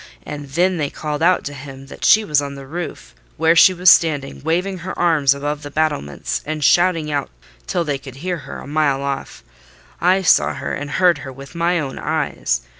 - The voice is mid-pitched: Yes, medium, 150 Hz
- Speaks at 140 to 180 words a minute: No, fast, 205 wpm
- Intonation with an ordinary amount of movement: Yes, average, 3.6 semitones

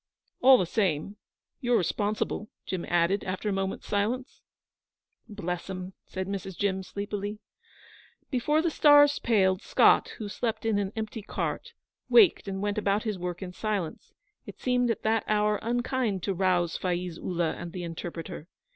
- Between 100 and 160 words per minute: Yes, average, 155 wpm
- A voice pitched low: No, high, 200 Hz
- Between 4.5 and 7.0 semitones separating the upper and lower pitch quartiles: No, average, 3.3 semitones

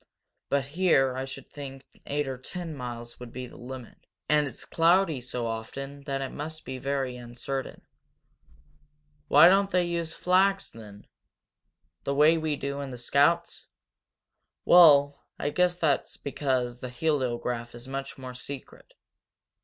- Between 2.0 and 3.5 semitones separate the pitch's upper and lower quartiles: No, average, 3.9 semitones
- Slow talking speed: No, average, 150 wpm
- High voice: No, medium, 140 Hz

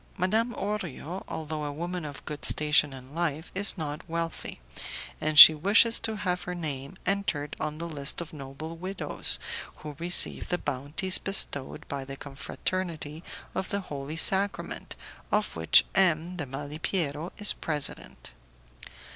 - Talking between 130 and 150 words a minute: Yes, average, 145 wpm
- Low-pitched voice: No, medium, 160 Hz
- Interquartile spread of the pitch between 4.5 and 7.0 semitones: No, average, 4.1 semitones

